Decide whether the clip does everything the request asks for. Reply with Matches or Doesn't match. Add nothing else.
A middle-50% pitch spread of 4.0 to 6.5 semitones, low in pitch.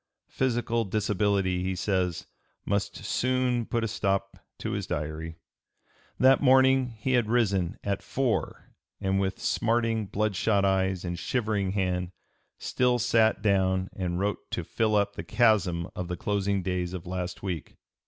Doesn't match